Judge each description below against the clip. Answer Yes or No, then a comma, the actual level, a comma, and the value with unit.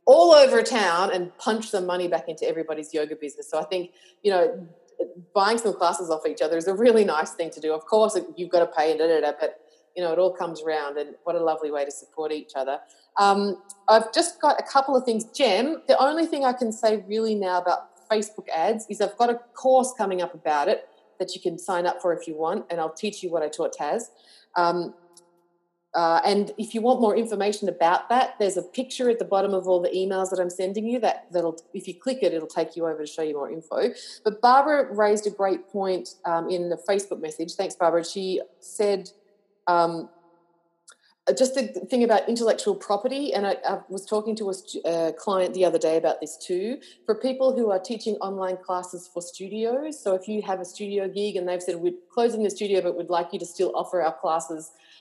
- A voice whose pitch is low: No, medium, 185 Hz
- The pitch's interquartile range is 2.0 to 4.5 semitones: Yes, average, 3.9 semitones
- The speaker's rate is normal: No, fast, 230 wpm